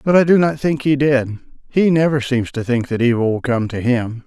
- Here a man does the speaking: Yes, male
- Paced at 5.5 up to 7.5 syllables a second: No, 5.1 syllables/s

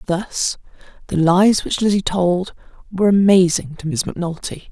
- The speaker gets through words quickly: No, average, 140 wpm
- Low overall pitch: No, medium, 185 Hz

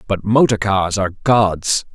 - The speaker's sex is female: No, male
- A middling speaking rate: Yes, average, 155 wpm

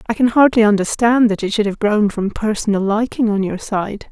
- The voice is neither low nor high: No, high, 215 Hz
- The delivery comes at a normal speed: No, fast, 220 wpm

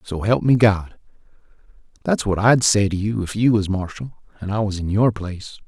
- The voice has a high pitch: No, low, 105 Hz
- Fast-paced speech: Yes, fast, 210 wpm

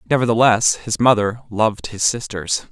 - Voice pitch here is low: Yes, low, 110 Hz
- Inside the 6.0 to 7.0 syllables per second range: No, 5.0 syllables/s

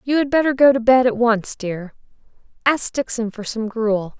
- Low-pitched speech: No, high, 235 Hz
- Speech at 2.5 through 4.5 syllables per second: No, 4.7 syllables/s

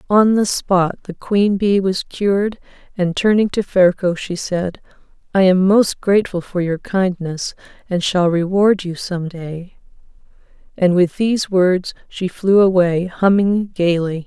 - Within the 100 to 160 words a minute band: Yes, average, 150 wpm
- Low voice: No, medium, 185 Hz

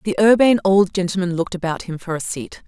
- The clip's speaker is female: Yes, female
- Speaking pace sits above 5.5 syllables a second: Yes, 6.5 syllables/s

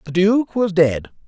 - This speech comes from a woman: No, male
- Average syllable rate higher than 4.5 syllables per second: No, 4.0 syllables/s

